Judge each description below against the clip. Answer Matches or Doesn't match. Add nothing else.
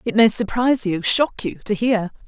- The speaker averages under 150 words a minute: Doesn't match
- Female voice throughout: Matches